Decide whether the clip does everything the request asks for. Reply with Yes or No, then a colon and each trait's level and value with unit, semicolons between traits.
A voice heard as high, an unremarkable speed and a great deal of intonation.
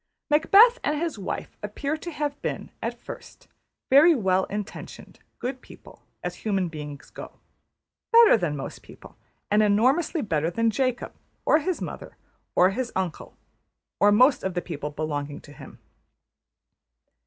Yes: high, 215 Hz; average, 145 wpm; wide, 8.8 semitones